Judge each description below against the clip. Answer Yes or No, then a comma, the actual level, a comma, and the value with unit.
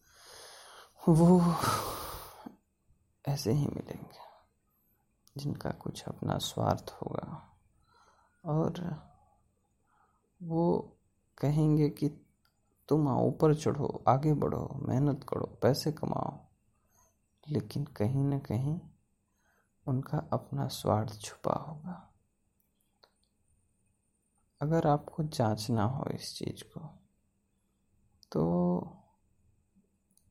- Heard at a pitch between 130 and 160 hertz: Yes, medium, 140 Hz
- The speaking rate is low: Yes, slow, 80 wpm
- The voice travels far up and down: Yes, wide, 6.6 semitones